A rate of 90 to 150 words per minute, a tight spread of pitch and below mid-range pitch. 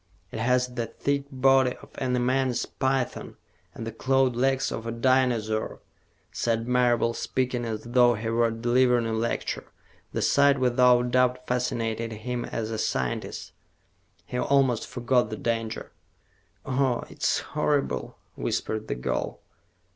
Yes: average, 140 wpm; narrow, 2.1 semitones; low, 125 Hz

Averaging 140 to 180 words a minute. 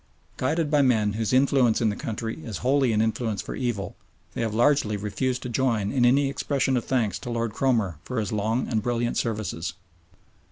No: average, 195 wpm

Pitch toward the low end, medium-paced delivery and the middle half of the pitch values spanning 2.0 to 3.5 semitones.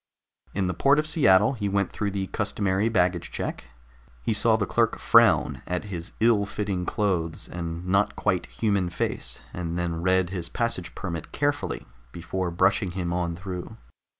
Yes: very low, 95 Hz; average, 165 wpm; average, 2.9 semitones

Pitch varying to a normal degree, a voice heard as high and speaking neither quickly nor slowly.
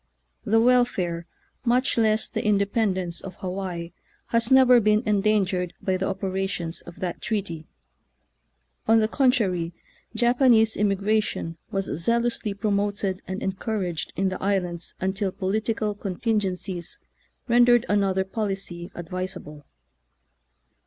No: average, 3.2 semitones; high, 195 Hz; slow, 120 wpm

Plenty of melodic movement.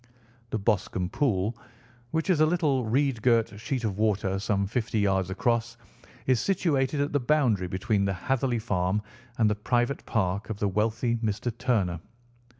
No: average, 4.3 semitones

